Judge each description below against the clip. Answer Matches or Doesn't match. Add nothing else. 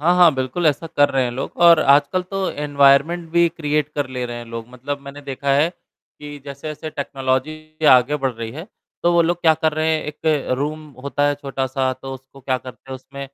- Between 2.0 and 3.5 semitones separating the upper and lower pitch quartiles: Matches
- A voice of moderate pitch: Matches